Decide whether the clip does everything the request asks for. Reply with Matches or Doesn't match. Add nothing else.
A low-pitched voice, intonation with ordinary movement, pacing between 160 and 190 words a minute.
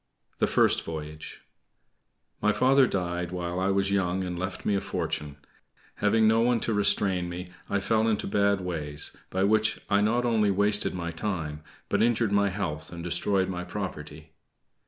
Matches